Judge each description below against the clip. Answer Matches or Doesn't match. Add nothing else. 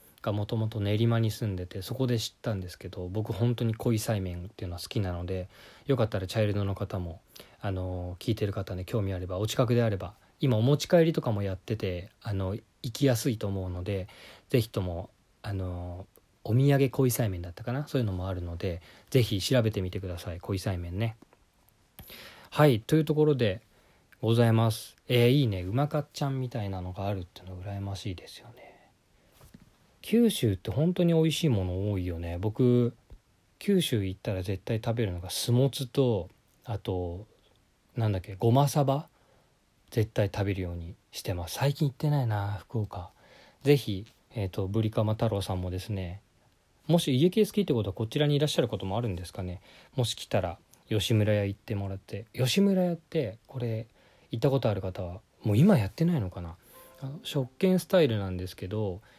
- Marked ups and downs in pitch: Doesn't match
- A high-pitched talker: Doesn't match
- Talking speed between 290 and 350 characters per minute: Doesn't match